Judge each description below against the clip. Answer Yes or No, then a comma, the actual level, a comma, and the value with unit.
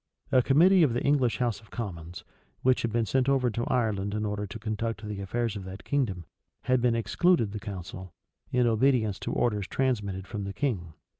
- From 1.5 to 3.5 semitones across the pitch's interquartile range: No, average, 3.9 semitones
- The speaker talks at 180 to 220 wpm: Yes, average, 200 wpm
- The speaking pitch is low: Yes, low, 110 Hz